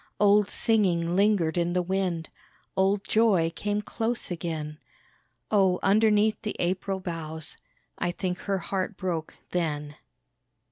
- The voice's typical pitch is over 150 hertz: Yes, medium, 185 Hz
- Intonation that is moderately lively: Yes, average, 3.4 semitones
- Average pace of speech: No, slow, 125 wpm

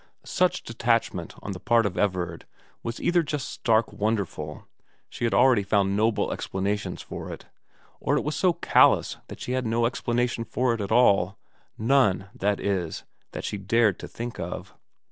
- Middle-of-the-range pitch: No, low, 110 Hz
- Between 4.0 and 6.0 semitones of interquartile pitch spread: No, average, 3.3 semitones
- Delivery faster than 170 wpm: No, average, 165 wpm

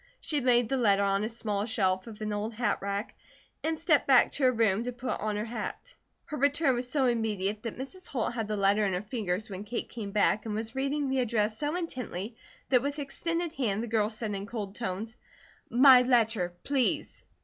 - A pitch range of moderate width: Yes, average, 4.0 semitones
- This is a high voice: Yes, high, 230 Hz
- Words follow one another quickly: Yes, fast, 210 wpm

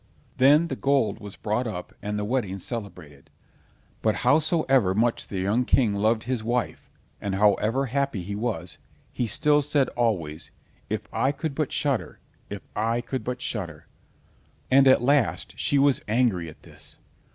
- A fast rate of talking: No, average, 155 wpm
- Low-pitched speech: Yes, low, 115 Hz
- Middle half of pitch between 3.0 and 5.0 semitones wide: Yes, average, 4.7 semitones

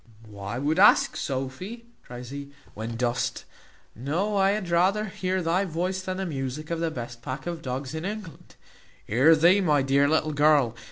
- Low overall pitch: No, medium, 155 Hz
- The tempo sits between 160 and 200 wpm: Yes, average, 175 wpm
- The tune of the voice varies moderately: No, wide, 6.0 semitones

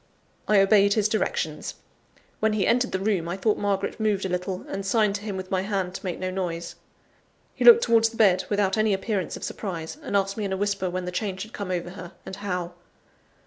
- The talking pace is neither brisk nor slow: No, fast, 225 wpm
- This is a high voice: Yes, high, 195 Hz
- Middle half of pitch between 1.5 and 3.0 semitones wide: Yes, narrow, 2.4 semitones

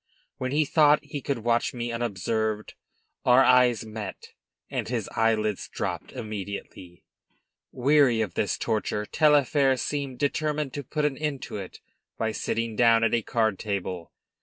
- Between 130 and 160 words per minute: Yes, average, 150 wpm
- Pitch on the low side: Yes, low, 120 Hz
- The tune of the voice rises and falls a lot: No, average, 4.5 semitones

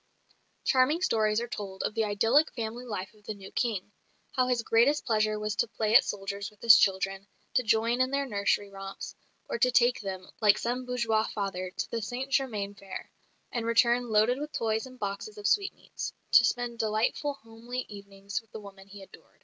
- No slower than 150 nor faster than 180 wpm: No, average, 195 wpm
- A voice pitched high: Yes, high, 220 Hz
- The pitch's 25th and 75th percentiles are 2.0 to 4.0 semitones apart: Yes, average, 3.3 semitones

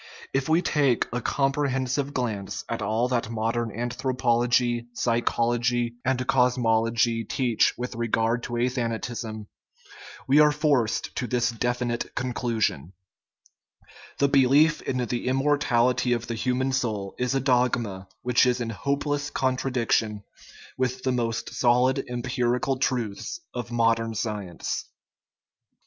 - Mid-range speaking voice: No, low, 120 Hz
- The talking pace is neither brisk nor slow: No, slow, 125 wpm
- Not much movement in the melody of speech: Yes, narrow, 2.0 semitones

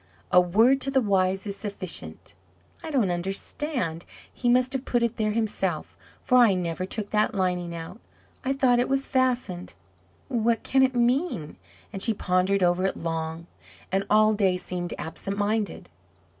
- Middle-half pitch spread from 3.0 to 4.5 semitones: No, average, 5.1 semitones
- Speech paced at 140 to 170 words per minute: Yes, average, 165 wpm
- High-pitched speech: Yes, high, 205 Hz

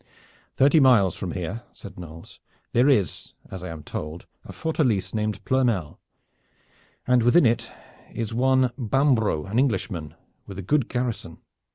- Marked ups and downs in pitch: Yes, wide, 5.9 semitones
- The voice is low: Yes, low, 110 Hz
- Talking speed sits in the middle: Yes, average, 145 wpm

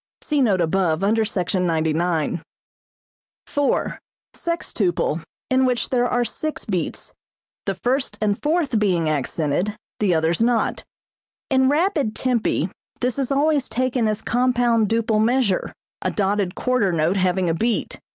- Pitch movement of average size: No, wide, 5.8 semitones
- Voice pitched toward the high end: Yes, high, 215 Hz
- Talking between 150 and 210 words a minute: No, slow, 135 wpm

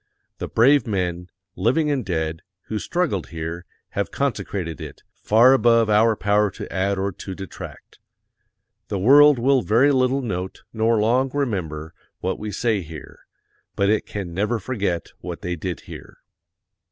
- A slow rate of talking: No, average, 155 wpm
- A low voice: Yes, low, 105 Hz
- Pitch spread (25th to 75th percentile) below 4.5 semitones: No, average, 5.1 semitones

